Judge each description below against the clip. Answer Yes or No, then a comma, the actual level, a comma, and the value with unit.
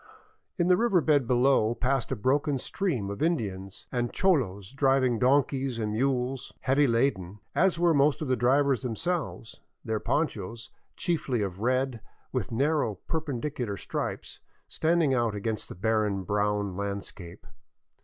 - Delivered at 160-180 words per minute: No, average, 145 wpm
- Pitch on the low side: Yes, low, 125 Hz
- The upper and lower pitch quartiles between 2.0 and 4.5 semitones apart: No, average, 5.1 semitones